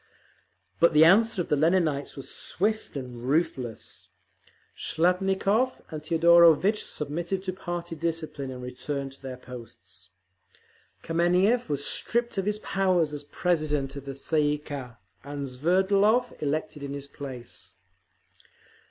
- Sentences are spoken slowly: Yes, slow, 130 wpm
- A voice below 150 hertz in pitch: No, medium, 155 Hz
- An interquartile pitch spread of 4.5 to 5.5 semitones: Yes, average, 4.9 semitones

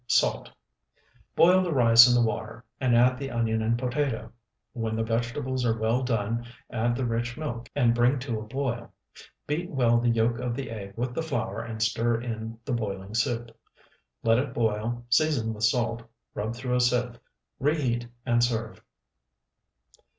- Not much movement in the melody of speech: Yes, narrow, 1.8 semitones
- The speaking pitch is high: No, low, 120 Hz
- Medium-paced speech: Yes, average, 170 wpm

